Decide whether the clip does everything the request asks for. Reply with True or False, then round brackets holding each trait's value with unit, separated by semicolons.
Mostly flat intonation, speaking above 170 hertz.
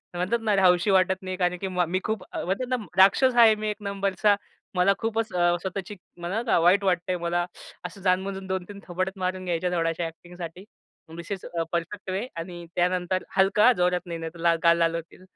True (2.2 semitones; 185 Hz)